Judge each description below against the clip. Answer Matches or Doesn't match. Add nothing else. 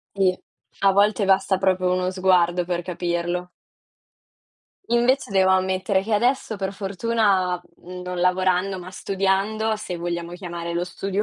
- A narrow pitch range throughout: Matches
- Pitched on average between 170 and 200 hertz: Matches